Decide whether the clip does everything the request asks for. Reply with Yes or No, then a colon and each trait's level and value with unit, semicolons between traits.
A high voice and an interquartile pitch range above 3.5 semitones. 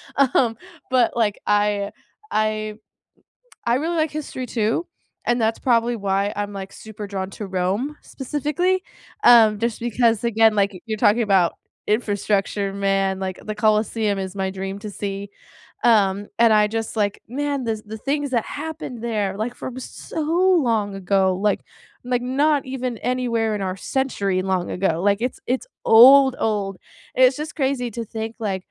Yes: high, 220 Hz; average, 3.9 semitones